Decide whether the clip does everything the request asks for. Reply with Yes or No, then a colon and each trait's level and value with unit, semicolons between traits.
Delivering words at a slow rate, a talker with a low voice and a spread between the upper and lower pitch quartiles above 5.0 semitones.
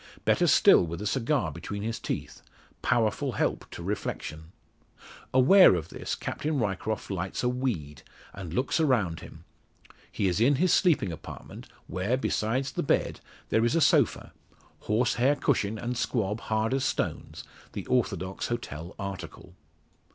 No: average, 145 wpm; low, 110 Hz; wide, 5.4 semitones